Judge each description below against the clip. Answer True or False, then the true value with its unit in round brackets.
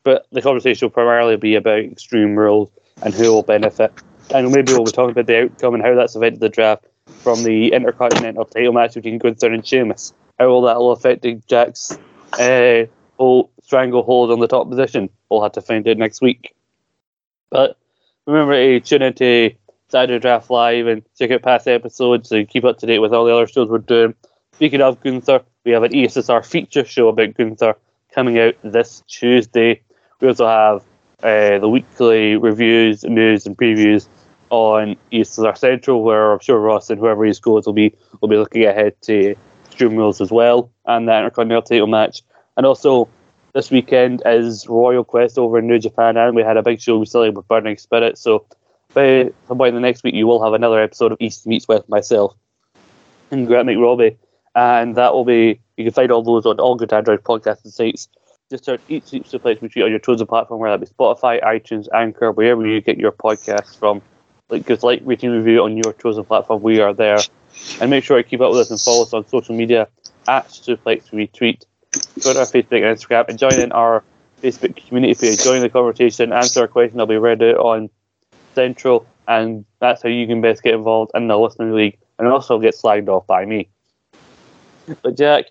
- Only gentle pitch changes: True (1.9 semitones)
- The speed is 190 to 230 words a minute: True (200 wpm)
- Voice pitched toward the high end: False (115 Hz)